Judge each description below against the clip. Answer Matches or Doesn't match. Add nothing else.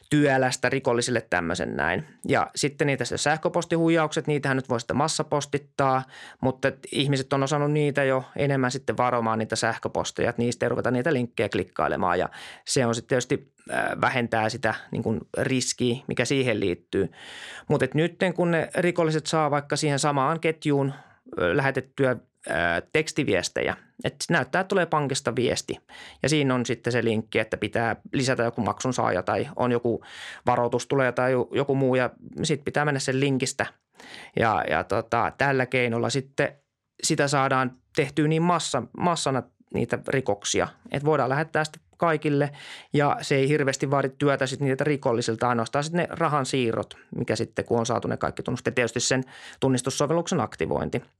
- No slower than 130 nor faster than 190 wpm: Matches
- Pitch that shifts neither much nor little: Matches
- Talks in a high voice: Doesn't match